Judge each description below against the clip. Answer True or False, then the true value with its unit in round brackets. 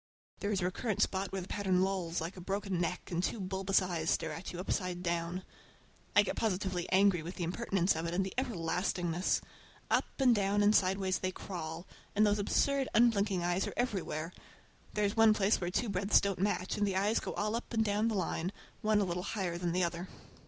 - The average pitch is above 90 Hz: True (190 Hz)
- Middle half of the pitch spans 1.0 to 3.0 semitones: True (2.6 semitones)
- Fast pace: True (215 wpm)